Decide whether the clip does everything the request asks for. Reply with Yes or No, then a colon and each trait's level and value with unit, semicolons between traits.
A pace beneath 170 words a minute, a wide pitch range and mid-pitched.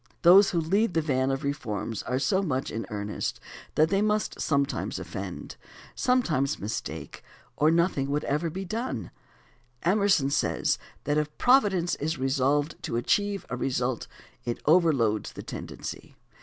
Yes: average, 150 wpm; wide, 6.2 semitones; medium, 150 Hz